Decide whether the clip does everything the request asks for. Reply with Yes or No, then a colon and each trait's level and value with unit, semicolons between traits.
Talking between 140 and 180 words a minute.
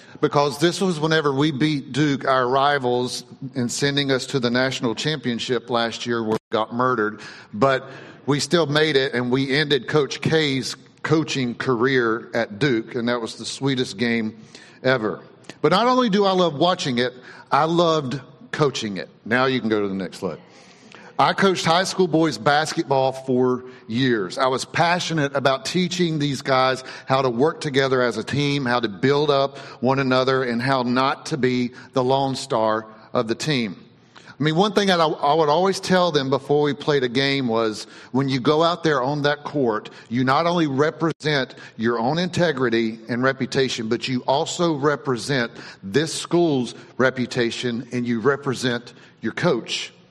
Yes: average, 175 wpm